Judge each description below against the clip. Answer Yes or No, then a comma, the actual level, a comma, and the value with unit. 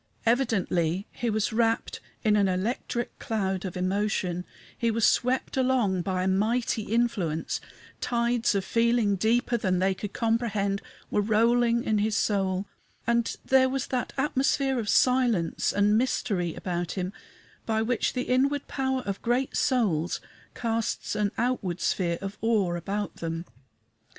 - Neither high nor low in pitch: No, high, 220 Hz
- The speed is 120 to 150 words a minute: Yes, average, 145 wpm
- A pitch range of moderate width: Yes, average, 4.0 semitones